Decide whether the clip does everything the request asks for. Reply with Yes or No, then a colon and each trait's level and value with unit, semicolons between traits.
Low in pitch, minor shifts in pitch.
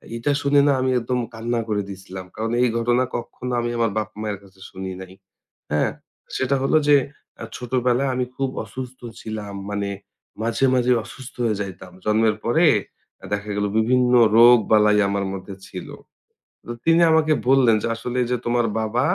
No: low, 115 Hz; average, 3.5 semitones